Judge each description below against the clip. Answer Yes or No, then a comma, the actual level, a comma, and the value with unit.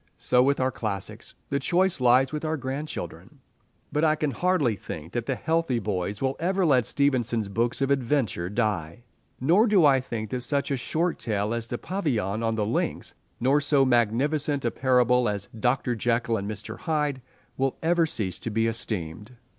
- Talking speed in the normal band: Yes, average, 180 wpm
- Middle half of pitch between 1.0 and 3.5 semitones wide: No, average, 4.5 semitones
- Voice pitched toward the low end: Yes, low, 125 Hz